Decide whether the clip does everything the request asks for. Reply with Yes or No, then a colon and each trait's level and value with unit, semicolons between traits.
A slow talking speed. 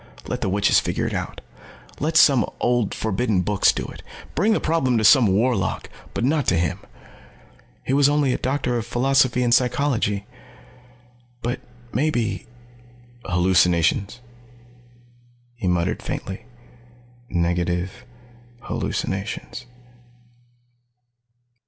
Yes: slow, 110 wpm